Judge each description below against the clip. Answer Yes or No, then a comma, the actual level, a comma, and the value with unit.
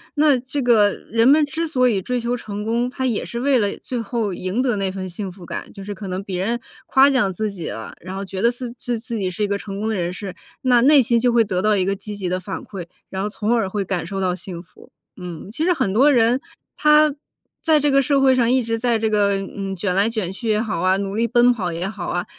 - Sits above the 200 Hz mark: Yes, high, 215 Hz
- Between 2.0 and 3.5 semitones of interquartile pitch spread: No, average, 4.2 semitones